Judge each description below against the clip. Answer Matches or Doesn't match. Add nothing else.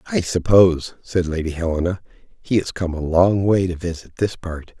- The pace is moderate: Matches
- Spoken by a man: Matches